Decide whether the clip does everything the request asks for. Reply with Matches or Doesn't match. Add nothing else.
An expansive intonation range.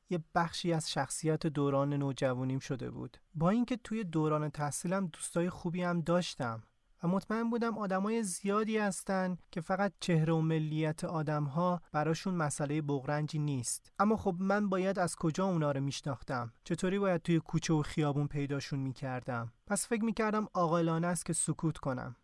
Doesn't match